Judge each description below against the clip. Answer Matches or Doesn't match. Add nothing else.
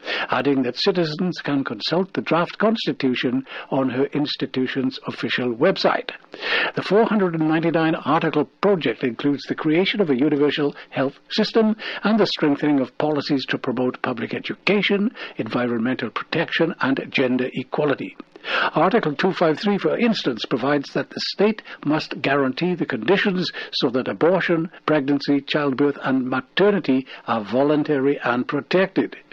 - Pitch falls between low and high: Matches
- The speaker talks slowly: Matches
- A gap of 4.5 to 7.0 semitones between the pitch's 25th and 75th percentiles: Matches